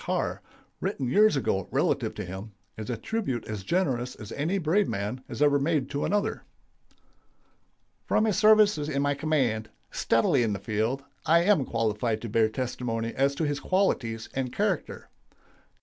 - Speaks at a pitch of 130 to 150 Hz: Yes, low, 135 Hz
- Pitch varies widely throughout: Yes, wide, 6.0 semitones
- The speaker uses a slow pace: No, average, 165 wpm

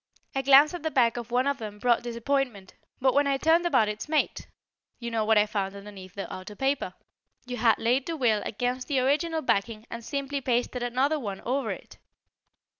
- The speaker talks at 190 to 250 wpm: Yes, average, 200 wpm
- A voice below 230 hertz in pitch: No, high, 245 Hz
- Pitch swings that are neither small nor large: Yes, average, 4.2 semitones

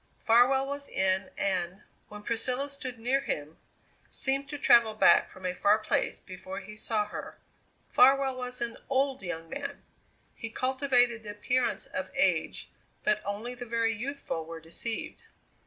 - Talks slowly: No, average, 155 wpm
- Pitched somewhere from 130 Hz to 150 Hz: No, high, 230 Hz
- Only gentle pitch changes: No, average, 4.6 semitones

